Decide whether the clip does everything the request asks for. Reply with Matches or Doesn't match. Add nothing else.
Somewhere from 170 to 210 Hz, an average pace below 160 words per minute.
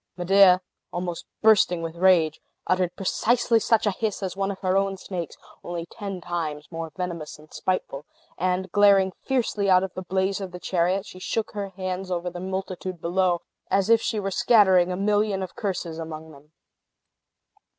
Doesn't match